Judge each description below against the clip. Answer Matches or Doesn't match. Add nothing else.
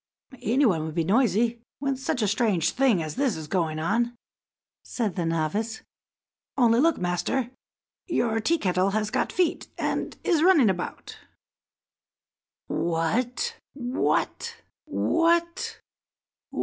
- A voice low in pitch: Doesn't match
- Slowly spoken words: Matches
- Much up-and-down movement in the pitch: Matches